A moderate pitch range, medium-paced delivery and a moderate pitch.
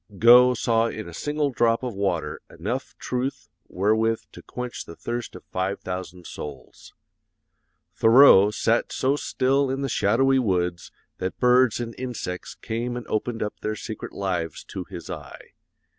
No: average, 4.4 semitones; average, 155 wpm; low, 115 Hz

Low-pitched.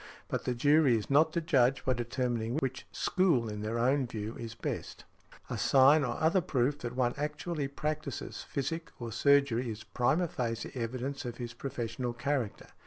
Yes: low, 130 Hz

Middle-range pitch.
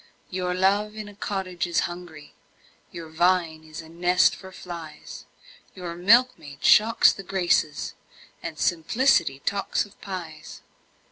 Yes: medium, 180 Hz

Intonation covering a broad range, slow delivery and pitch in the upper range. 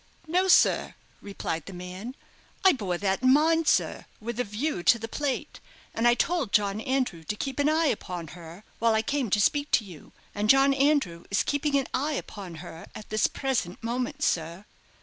No: wide, 6.4 semitones; average, 195 wpm; high, 230 Hz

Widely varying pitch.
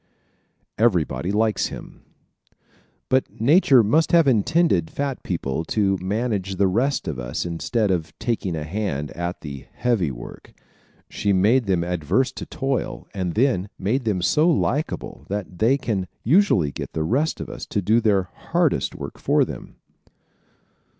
Yes: wide, 6.1 semitones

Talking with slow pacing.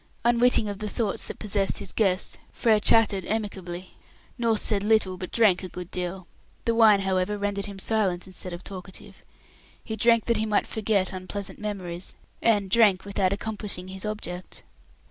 No: average, 165 wpm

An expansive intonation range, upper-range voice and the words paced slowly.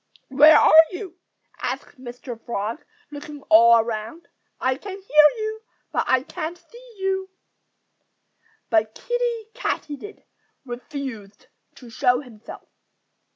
Yes: wide, 8.2 semitones; very high, 290 Hz; slow, 110 wpm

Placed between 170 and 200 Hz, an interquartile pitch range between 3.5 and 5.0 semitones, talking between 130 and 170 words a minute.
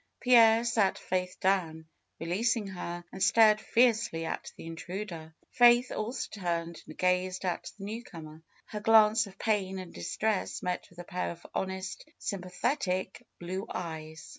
Yes: high, 190 Hz; average, 3.9 semitones; average, 145 wpm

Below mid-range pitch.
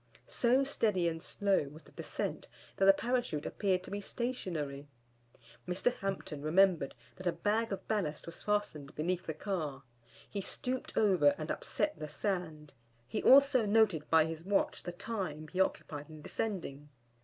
No: medium, 185 Hz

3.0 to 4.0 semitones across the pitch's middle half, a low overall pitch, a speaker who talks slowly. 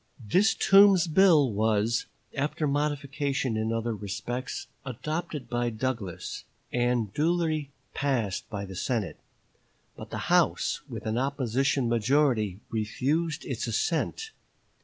No: average, 5.0 semitones; low, 130 Hz; slow, 115 wpm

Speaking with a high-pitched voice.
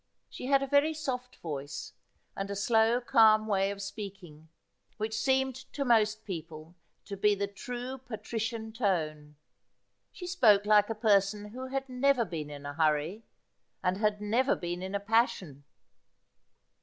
Yes: high, 210 Hz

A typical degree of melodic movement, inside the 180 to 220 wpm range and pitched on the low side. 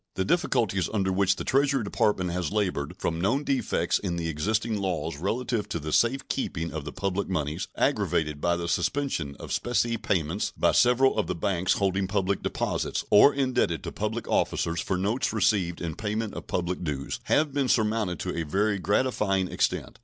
Yes: average, 4.7 semitones; average, 185 wpm; low, 100 Hz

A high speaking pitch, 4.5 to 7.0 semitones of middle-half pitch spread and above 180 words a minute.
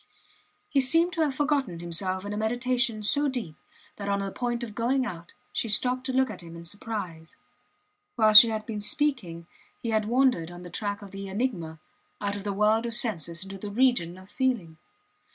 Yes: high, 215 Hz; average, 5.0 semitones; average, 200 wpm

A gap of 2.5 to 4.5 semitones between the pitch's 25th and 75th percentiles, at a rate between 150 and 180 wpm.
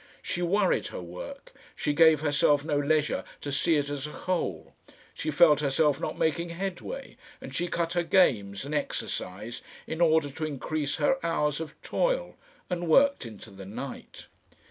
Yes: average, 3.5 semitones; average, 165 wpm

